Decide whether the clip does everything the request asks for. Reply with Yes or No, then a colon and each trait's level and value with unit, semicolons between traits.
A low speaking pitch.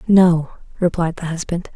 No: medium, 170 Hz